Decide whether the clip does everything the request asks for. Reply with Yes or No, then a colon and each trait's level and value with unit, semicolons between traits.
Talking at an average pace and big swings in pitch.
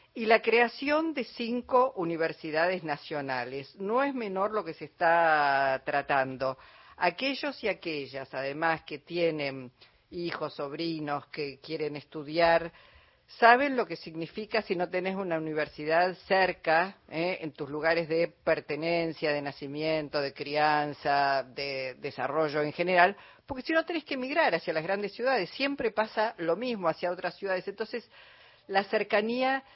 Yes: average, 140 wpm; wide, 6.3 semitones